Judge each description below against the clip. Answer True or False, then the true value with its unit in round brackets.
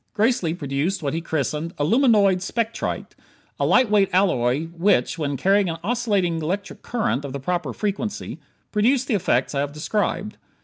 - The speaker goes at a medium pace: True (160 wpm)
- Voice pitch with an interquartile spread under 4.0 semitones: False (5.6 semitones)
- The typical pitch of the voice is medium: True (180 Hz)